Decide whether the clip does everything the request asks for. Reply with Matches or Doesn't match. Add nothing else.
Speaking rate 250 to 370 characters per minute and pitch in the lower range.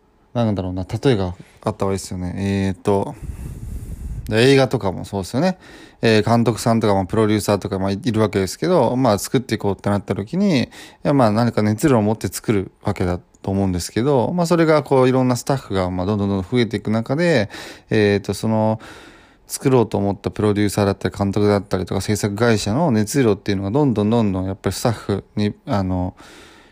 Doesn't match